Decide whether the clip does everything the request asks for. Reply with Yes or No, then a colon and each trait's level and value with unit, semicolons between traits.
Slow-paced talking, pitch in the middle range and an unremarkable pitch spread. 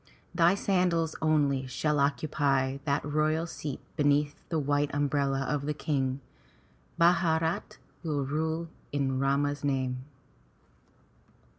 No: slow, 110 wpm; medium, 145 Hz; narrow, 2.3 semitones